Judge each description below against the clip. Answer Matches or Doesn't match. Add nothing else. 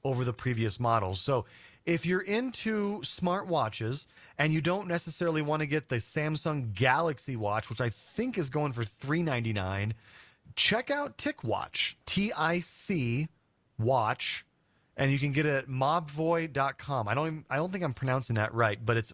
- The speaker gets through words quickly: Doesn't match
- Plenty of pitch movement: Matches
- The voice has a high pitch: Doesn't match